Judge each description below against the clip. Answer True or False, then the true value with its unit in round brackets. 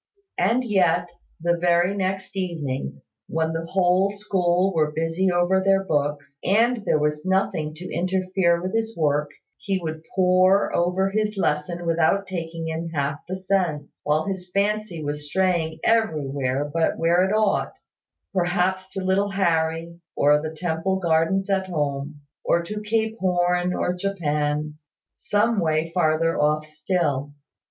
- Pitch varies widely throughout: False (3.4 semitones)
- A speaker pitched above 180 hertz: False (175 Hz)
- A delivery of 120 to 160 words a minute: True (145 wpm)